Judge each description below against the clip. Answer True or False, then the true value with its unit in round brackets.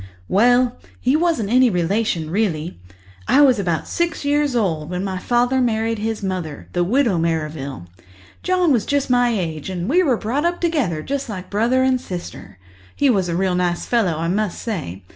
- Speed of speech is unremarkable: True (180 wpm)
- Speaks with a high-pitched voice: True (215 Hz)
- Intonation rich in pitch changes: True (6.6 semitones)